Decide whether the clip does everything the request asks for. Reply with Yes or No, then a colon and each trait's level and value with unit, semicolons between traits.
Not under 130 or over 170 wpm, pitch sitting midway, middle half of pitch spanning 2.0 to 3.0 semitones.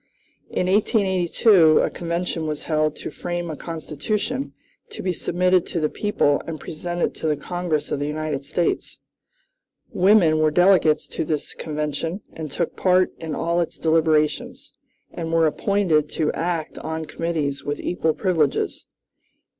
Yes: average, 145 wpm; medium, 165 Hz; narrow, 2.6 semitones